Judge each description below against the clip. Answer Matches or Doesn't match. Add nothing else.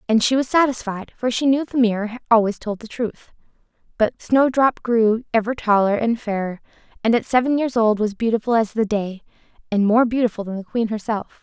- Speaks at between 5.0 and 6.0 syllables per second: Matches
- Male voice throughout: Doesn't match